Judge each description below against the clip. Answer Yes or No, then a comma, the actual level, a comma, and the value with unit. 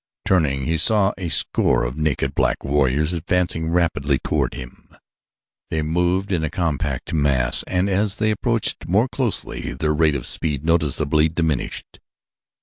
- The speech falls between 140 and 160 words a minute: Yes, average, 145 wpm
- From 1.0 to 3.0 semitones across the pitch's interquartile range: No, average, 3.9 semitones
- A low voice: Yes, very low, 80 Hz